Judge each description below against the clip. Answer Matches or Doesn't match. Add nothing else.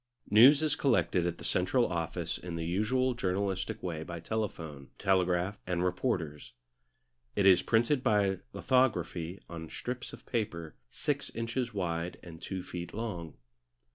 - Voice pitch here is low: Matches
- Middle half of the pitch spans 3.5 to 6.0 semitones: Matches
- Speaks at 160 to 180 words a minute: Doesn't match